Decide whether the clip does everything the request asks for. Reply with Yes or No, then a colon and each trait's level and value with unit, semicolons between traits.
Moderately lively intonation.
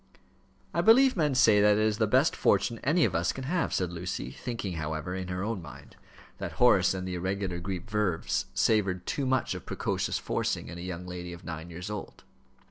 Yes: average, 4.6 semitones